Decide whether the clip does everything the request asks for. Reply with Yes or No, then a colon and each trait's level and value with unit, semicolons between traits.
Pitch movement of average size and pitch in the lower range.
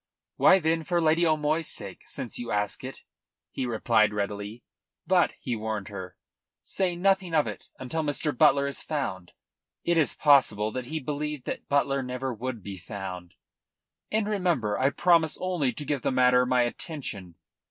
No: wide, 6.5 semitones; low, 130 Hz